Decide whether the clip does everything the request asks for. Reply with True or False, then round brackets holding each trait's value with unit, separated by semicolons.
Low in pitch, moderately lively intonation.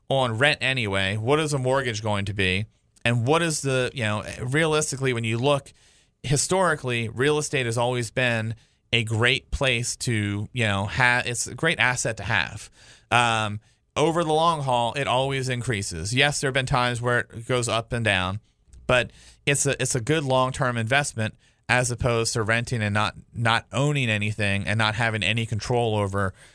True (120 Hz; 3.5 semitones)